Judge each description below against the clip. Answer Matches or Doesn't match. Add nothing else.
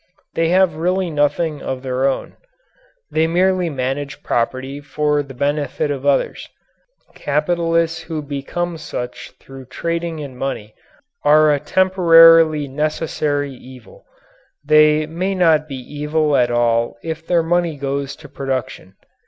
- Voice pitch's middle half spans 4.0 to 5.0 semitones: Doesn't match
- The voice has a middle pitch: Matches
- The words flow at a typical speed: Doesn't match